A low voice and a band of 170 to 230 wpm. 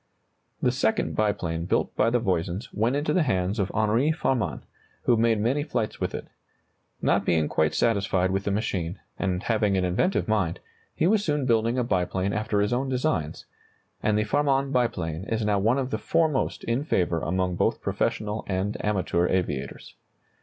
Yes: low, 105 Hz; average, 175 wpm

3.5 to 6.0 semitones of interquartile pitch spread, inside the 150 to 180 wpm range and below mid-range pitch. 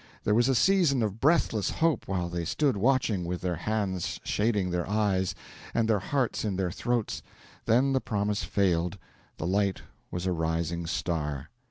Yes: average, 4.8 semitones; average, 170 wpm; low, 100 Hz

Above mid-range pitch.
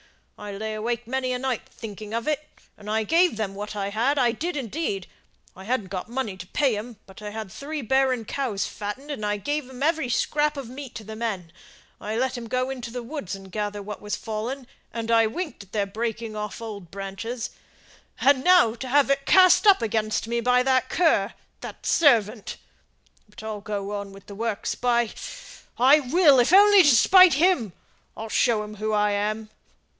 Yes: high, 230 Hz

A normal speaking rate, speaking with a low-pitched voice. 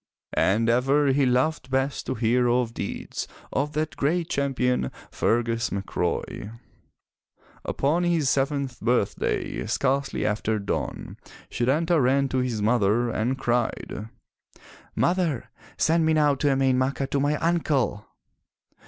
No: slow, 125 wpm; low, 130 Hz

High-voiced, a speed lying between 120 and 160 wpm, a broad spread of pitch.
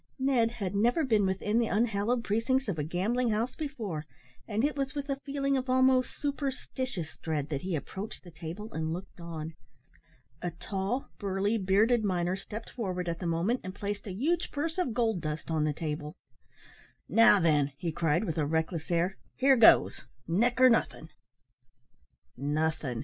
No: high, 200 Hz; average, 170 wpm; wide, 6.7 semitones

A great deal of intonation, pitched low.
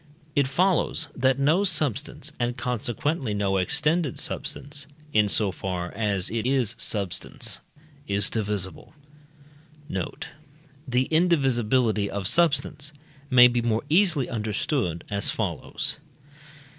Yes: wide, 5.8 semitones; low, 120 Hz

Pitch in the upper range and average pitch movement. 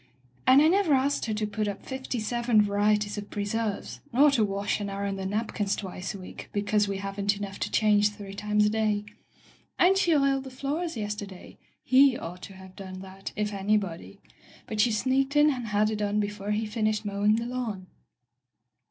Yes: high, 210 Hz; average, 3.1 semitones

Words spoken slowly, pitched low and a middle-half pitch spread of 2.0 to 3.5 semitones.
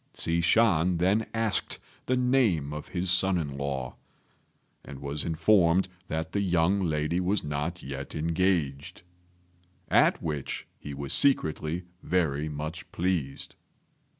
No: slow, 125 wpm; very low, 85 Hz; average, 4.0 semitones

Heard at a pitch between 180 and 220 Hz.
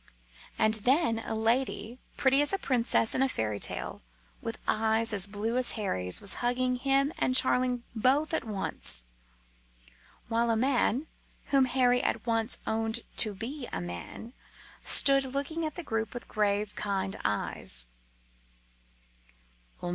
No: high, 230 Hz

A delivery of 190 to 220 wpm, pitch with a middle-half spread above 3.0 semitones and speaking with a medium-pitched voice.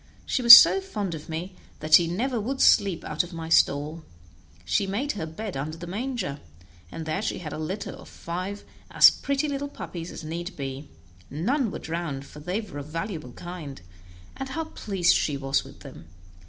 Yes: average, 195 wpm; wide, 5.6 semitones; medium, 175 Hz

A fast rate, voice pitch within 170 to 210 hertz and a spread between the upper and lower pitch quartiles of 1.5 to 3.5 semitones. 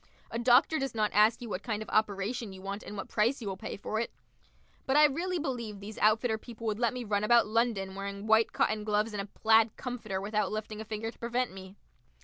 No: fast, 235 wpm; high, 220 Hz; narrow, 2.4 semitones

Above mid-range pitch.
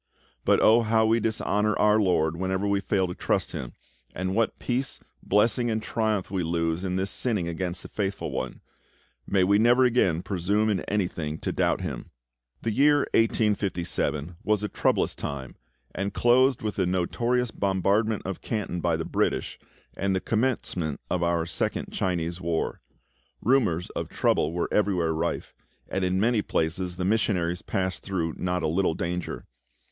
No: very low, 95 Hz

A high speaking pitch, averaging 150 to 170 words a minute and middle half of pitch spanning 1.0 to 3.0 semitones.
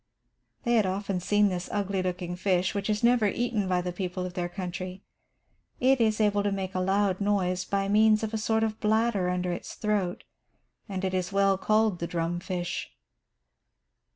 No: high, 195 Hz; average, 185 wpm; narrow, 2.6 semitones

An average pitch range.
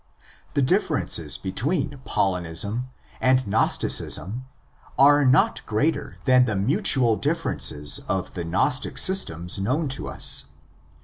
No: wide, 6.8 semitones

